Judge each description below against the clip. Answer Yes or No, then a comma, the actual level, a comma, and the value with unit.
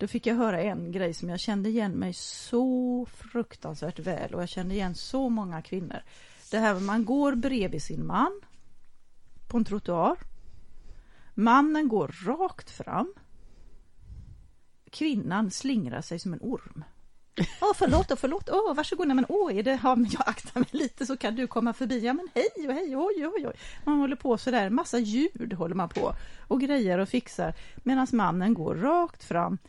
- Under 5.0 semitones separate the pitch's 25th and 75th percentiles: No, wide, 5.5 semitones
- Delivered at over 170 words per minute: Yes, average, 185 wpm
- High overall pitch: Yes, high, 240 Hz